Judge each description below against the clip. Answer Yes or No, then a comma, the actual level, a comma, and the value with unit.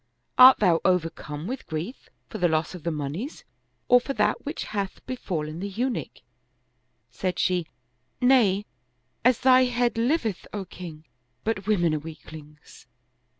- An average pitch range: No, wide, 7.2 semitones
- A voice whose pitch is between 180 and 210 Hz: Yes, high, 190 Hz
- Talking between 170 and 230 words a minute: No, average, 150 wpm